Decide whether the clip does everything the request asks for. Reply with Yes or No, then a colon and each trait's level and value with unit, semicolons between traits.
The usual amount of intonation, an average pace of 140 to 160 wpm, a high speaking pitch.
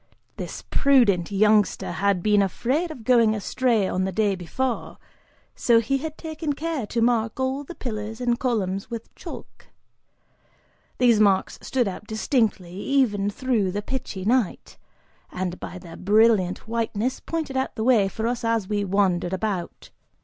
Yes: average, 4.3 semitones; average, 155 wpm; high, 220 Hz